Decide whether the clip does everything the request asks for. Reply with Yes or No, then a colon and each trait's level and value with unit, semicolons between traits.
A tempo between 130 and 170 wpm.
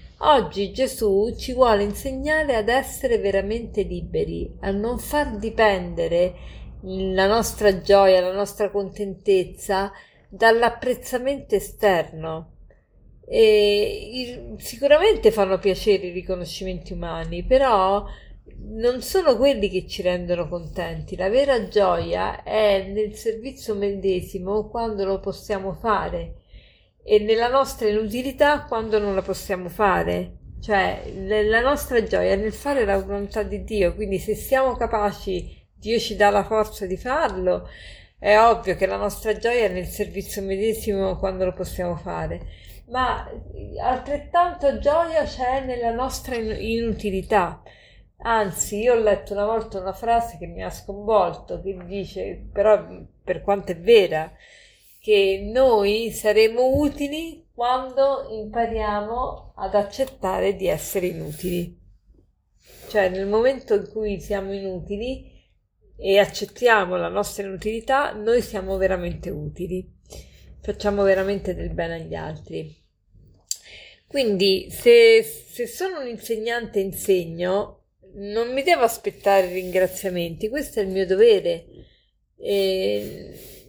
No: average, 120 wpm